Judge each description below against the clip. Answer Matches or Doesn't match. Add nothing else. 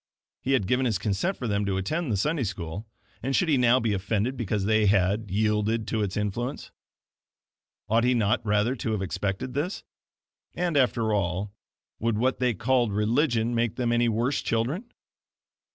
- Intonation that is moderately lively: Matches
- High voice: Doesn't match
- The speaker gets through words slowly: Doesn't match